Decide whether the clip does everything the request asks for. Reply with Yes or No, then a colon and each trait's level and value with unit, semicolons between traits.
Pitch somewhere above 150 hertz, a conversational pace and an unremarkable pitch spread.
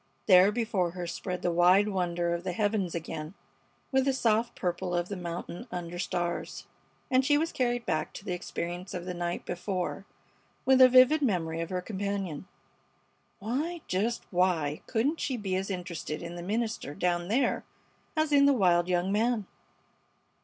Yes: medium, 185 Hz; average, 170 wpm; average, 4.9 semitones